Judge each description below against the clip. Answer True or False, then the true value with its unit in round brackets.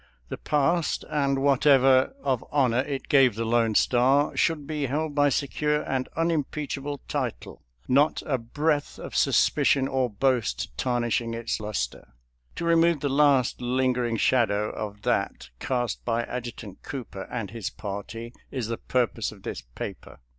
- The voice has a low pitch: True (130 Hz)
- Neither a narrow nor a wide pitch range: True (3.8 semitones)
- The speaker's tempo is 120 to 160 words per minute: True (155 wpm)